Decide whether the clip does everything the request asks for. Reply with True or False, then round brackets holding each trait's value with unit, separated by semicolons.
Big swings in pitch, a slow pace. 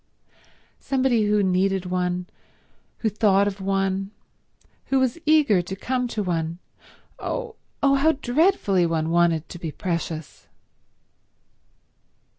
True (6.1 semitones; 110 wpm)